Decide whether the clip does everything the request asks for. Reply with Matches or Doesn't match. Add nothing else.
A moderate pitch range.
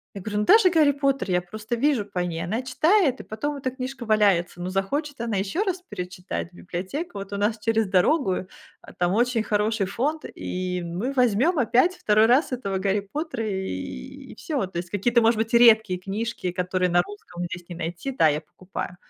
Doesn't match